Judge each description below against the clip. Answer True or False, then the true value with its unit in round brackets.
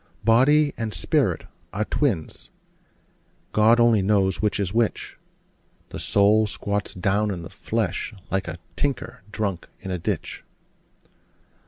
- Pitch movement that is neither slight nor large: True (3.1 semitones)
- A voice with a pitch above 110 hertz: False (105 Hz)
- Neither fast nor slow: False (130 wpm)